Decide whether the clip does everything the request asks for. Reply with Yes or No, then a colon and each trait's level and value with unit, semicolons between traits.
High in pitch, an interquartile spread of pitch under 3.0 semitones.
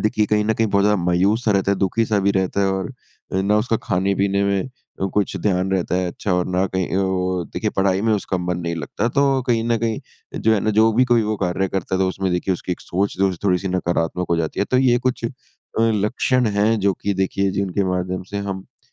No: low, 100 Hz; narrow, 2.6 semitones